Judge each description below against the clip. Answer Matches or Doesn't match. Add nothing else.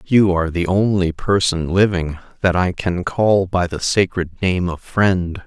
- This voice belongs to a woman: Doesn't match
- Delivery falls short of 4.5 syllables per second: Matches